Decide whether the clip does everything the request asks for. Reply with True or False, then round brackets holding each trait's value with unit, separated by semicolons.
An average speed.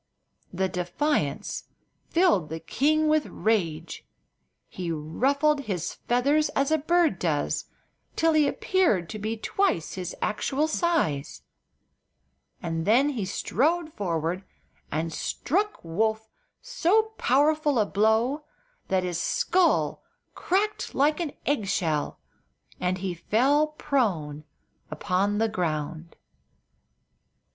False (110 wpm)